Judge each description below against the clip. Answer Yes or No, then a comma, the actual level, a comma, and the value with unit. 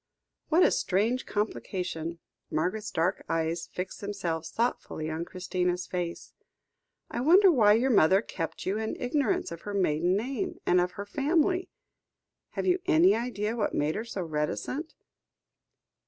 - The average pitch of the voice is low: No, high, 200 Hz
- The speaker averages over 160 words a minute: No, average, 145 wpm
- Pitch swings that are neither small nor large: No, wide, 6.1 semitones